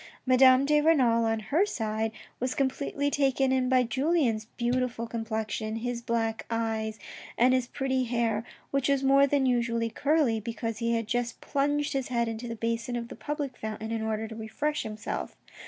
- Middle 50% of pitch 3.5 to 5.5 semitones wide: No, average, 3.1 semitones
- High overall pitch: Yes, high, 240 Hz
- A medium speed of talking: Yes, average, 180 wpm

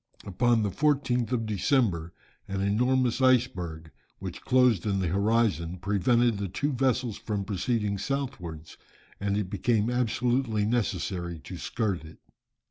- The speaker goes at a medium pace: No, slow, 130 wpm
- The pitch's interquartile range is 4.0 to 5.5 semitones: Yes, average, 4.5 semitones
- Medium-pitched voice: No, low, 105 Hz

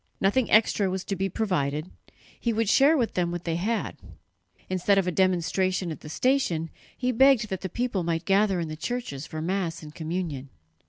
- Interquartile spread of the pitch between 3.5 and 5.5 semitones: Yes, average, 4.6 semitones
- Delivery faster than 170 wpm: Yes, average, 195 wpm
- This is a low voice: No, medium, 185 Hz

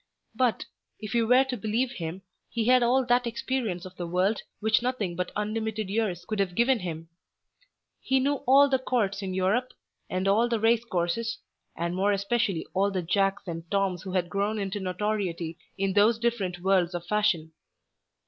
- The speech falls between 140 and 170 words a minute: No, average, 180 wpm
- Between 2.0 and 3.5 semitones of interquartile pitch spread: No, average, 4.2 semitones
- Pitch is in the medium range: No, high, 205 Hz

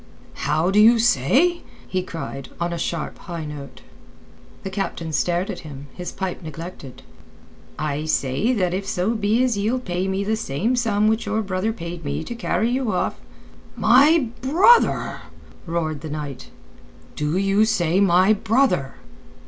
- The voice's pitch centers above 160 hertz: Yes, high, 190 Hz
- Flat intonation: No, wide, 5.6 semitones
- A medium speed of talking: Yes, average, 155 wpm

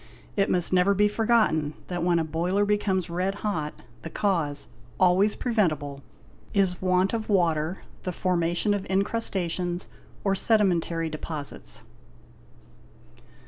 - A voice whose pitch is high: No, medium, 180 Hz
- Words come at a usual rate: No, slow, 115 wpm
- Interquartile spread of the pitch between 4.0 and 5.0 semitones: No, average, 3.4 semitones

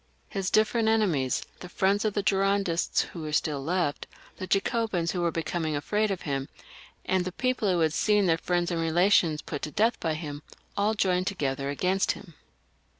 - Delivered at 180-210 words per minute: Yes, average, 185 wpm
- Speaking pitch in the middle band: Yes, medium, 180 Hz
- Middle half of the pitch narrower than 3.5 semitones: No, average, 4.1 semitones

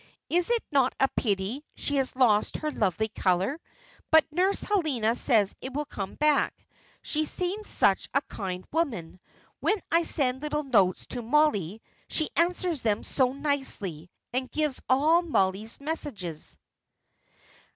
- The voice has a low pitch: No, very high, 270 Hz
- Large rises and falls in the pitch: Yes, wide, 6.7 semitones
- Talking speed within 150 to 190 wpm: No, average, 140 wpm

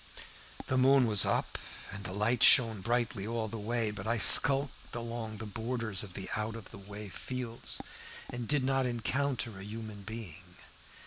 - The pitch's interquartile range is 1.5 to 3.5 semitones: Yes, average, 2.7 semitones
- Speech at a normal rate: Yes, average, 170 wpm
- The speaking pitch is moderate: No, low, 115 Hz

